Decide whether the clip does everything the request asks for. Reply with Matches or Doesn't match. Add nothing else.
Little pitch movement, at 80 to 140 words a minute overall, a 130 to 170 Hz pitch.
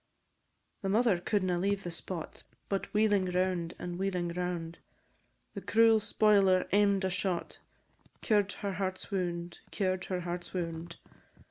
Doesn't match